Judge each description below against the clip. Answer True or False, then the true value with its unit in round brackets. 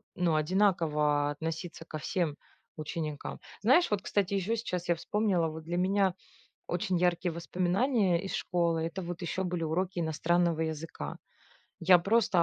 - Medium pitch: True (175 Hz)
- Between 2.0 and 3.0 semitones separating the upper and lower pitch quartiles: True (2.7 semitones)